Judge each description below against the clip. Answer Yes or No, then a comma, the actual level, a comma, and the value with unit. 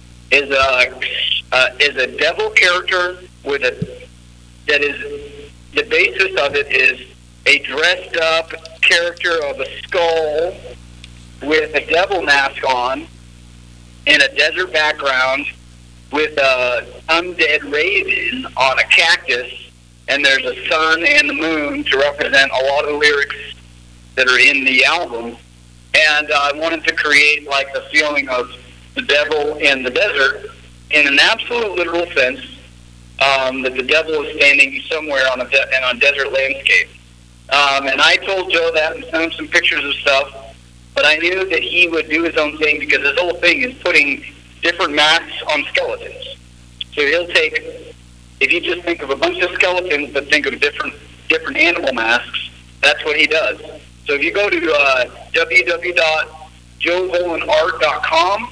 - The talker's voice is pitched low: No, medium, 145 Hz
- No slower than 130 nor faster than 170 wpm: Yes, average, 160 wpm